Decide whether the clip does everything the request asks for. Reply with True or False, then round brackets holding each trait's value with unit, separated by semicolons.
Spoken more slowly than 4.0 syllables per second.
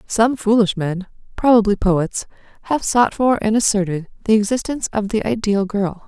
False (5.0 syllables/s)